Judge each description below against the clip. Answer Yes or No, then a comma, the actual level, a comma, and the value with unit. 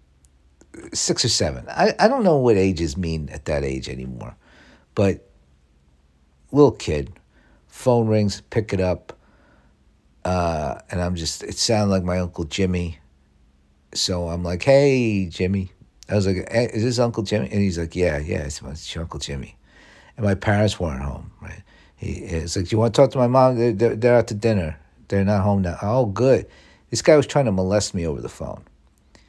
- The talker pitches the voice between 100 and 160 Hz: No, very low, 90 Hz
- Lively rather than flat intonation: Yes, wide, 6.9 semitones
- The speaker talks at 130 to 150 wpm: No, average, 185 wpm